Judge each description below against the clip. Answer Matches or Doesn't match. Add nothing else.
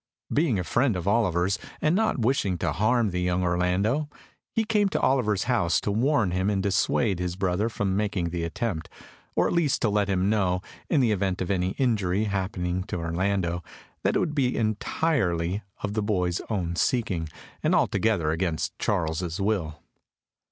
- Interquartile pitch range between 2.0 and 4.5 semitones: Matches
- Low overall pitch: Matches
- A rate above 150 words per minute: Matches